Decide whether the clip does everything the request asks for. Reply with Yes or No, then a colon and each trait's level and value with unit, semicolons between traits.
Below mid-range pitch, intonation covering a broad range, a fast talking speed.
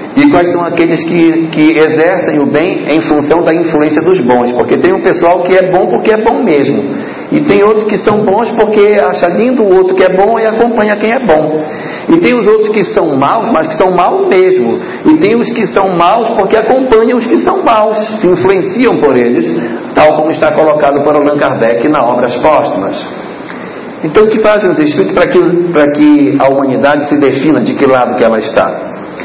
No: medium, 180 Hz; wide, 6.0 semitones; fast, 210 wpm